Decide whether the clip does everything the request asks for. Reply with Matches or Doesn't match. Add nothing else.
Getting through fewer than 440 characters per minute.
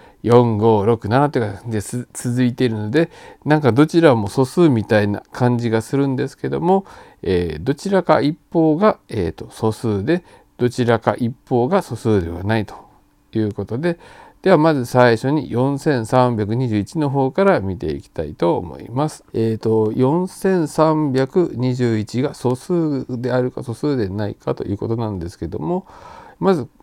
Matches